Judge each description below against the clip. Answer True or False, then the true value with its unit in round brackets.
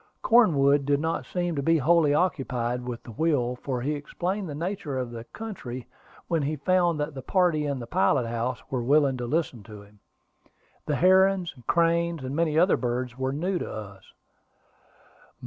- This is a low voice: False (145 Hz)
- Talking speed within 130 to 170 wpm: False (180 wpm)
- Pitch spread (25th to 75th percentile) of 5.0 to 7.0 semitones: True (5.3 semitones)